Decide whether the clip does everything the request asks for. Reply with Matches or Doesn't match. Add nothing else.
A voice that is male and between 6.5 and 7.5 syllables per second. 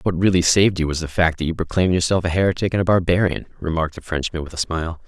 Matches